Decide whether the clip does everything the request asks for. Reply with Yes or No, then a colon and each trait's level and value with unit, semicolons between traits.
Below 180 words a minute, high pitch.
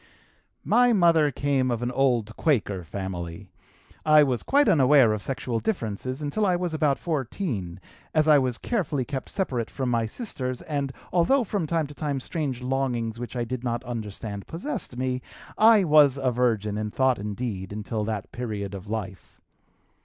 No: average, 170 wpm; low, 130 Hz